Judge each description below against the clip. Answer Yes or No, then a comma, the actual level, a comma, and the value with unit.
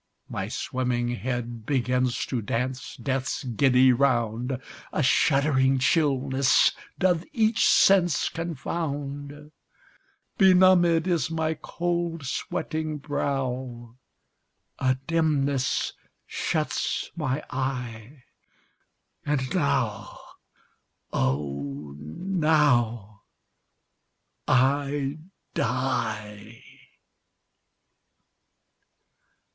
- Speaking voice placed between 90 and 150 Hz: Yes, low, 135 Hz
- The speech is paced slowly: Yes, slow, 65 wpm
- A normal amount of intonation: Yes, average, 4.0 semitones